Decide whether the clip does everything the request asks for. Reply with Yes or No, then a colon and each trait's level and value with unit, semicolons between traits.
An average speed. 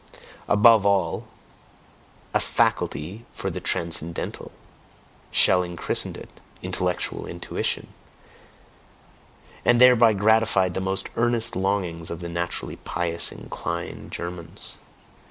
No: slow, 100 wpm